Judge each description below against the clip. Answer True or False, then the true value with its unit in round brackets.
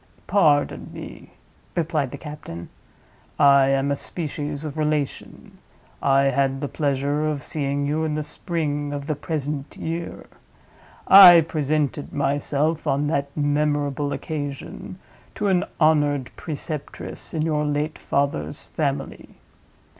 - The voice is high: False (145 Hz)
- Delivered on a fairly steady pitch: True (1.7 semitones)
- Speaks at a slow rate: True (125 wpm)